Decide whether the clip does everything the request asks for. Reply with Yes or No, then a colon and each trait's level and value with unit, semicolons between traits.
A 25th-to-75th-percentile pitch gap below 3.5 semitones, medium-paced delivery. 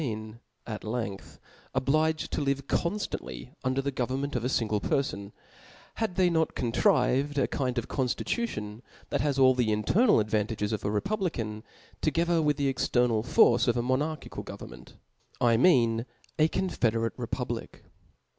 No: average, 4.9 semitones; average, 155 wpm